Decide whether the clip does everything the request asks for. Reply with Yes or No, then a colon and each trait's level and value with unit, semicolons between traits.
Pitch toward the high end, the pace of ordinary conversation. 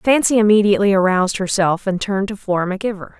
Yes: high, 200 Hz; average, 190 wpm